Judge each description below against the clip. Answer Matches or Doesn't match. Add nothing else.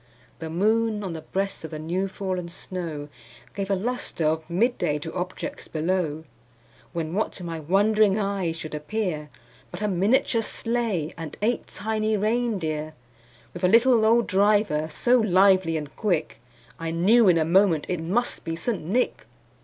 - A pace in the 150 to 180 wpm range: Matches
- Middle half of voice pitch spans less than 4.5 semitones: Doesn't match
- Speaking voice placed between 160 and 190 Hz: Matches